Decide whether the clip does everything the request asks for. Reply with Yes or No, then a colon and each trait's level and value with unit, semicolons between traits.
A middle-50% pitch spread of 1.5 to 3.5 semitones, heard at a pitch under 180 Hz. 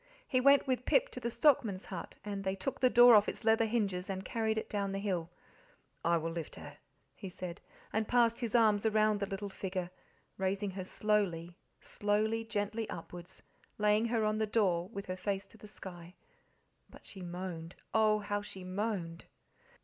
No: average, 3.1 semitones; high, 205 Hz